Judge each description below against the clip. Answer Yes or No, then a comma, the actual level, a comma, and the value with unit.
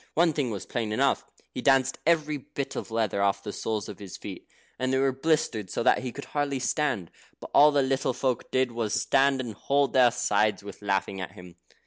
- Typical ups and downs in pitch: Yes, average, 4.8 semitones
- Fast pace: Yes, fast, 220 wpm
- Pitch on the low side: Yes, low, 125 Hz